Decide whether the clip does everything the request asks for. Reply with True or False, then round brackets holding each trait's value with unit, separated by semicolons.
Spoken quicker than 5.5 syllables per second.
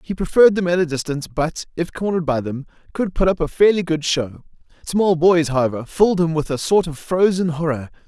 True (5.8 syllables/s)